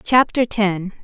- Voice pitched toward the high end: Yes, high, 210 Hz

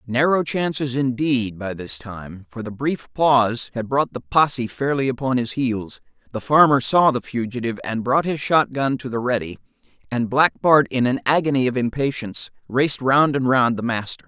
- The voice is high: No, low, 125 Hz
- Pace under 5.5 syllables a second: Yes, 5.0 syllables/s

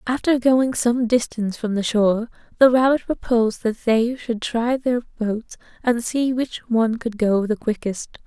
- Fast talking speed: No, average, 175 wpm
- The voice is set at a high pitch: Yes, high, 235 Hz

